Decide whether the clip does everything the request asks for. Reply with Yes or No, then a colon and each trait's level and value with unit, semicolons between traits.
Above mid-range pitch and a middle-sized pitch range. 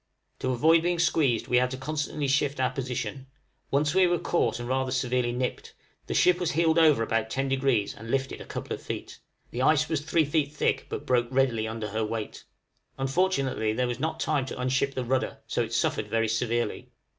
No: low, 130 Hz; average, 3.7 semitones